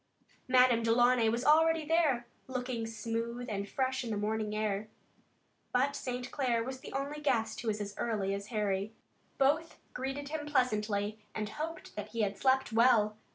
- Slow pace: No, average, 170 wpm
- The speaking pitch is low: No, high, 235 Hz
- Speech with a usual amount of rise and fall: Yes, average, 3.7 semitones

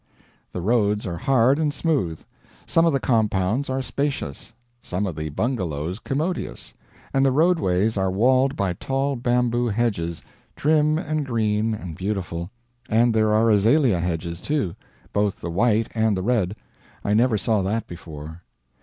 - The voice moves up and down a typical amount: No, wide, 6.1 semitones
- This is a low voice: Yes, low, 110 Hz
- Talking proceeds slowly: No, average, 155 wpm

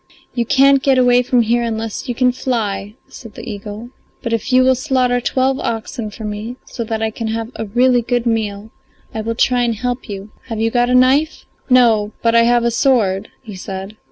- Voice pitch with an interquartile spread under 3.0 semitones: Yes, narrow, 2.4 semitones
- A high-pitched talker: Yes, high, 235 Hz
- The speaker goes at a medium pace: No, fast, 215 wpm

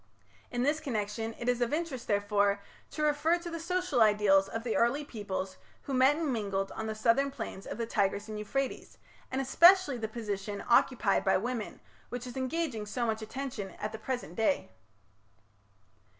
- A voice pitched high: Yes, high, 235 Hz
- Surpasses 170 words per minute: Yes, average, 180 wpm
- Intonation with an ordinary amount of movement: Yes, average, 4.6 semitones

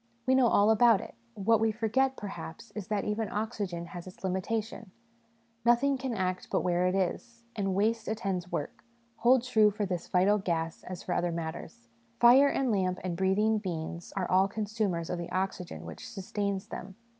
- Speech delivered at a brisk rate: No, average, 185 wpm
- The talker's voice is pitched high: Yes, high, 200 Hz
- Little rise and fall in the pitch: No, average, 3.6 semitones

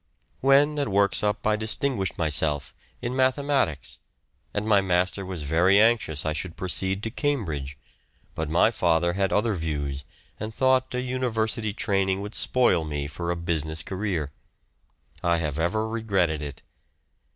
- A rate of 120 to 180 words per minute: Yes, average, 145 wpm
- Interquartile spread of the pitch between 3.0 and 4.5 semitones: No, wide, 5.6 semitones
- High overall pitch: No, very low, 95 Hz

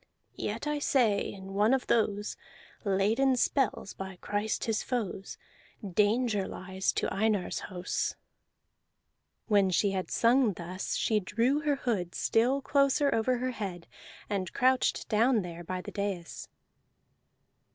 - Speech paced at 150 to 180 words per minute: No, slow, 135 wpm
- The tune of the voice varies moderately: Yes, average, 4.6 semitones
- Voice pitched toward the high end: Yes, high, 210 Hz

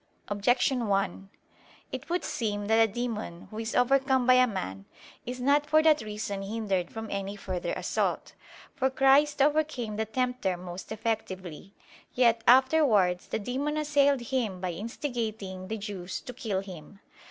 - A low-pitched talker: No, high, 225 Hz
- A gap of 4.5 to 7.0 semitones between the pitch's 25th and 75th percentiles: Yes, average, 4.9 semitones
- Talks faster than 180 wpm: No, average, 155 wpm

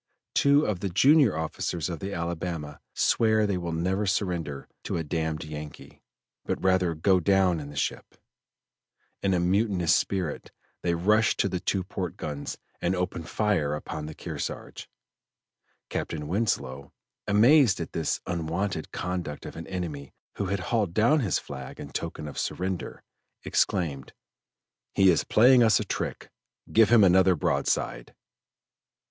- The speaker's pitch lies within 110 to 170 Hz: No, very low, 90 Hz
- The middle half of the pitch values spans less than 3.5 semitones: No, average, 3.8 semitones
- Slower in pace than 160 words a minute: Yes, average, 150 wpm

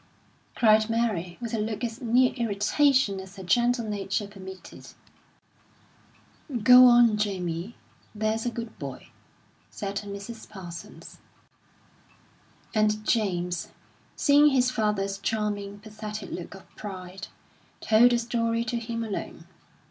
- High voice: Yes, high, 215 Hz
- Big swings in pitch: No, average, 3.1 semitones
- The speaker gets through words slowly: Yes, slow, 120 wpm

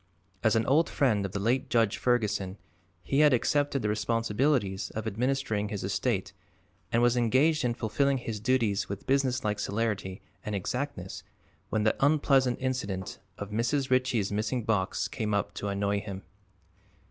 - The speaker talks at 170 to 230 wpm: No, average, 155 wpm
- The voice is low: Yes, low, 115 Hz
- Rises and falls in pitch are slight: No, average, 4.2 semitones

